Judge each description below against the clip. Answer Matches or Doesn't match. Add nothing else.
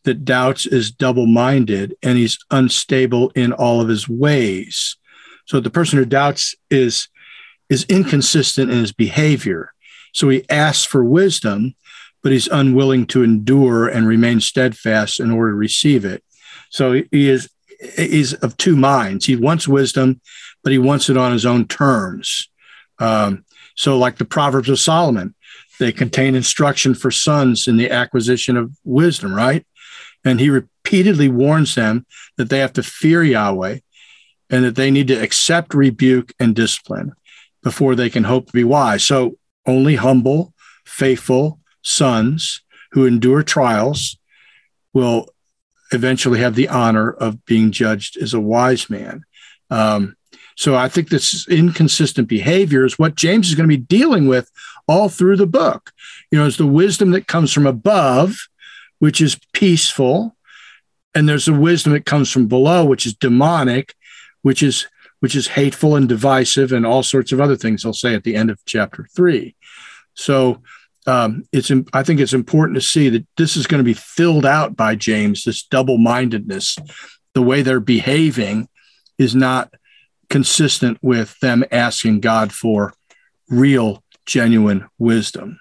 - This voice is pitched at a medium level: Doesn't match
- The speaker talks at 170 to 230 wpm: Doesn't match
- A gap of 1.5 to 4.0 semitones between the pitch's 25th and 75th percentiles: Matches